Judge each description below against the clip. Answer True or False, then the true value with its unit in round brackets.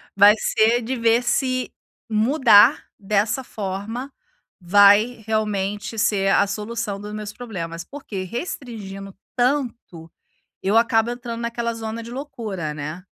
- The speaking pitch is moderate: False (220 Hz)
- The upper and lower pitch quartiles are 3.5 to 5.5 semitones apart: False (3.1 semitones)